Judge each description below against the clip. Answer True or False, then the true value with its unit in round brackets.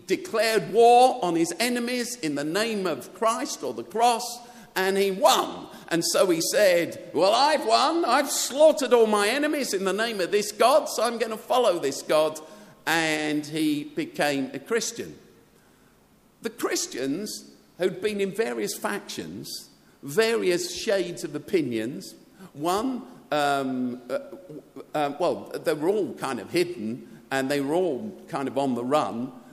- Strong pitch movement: True (7.0 semitones)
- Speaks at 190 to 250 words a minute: False (155 wpm)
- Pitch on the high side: True (210 Hz)